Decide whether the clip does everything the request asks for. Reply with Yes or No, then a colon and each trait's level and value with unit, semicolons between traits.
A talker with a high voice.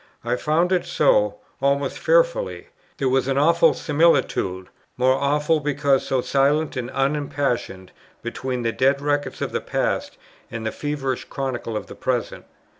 No: low, 135 Hz